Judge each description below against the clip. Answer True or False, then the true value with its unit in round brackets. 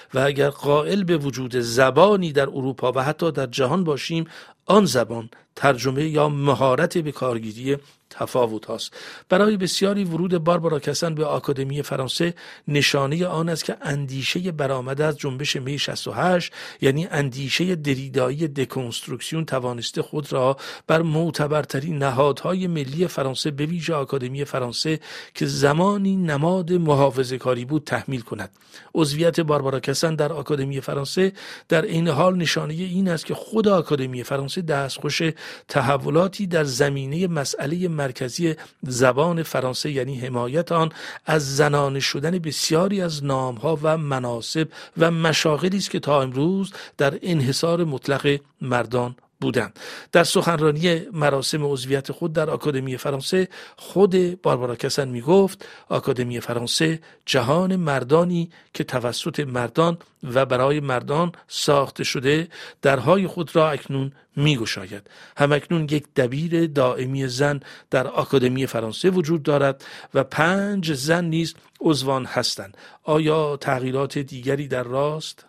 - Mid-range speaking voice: True (145 Hz)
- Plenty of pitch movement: False (3.7 semitones)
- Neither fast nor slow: True (130 wpm)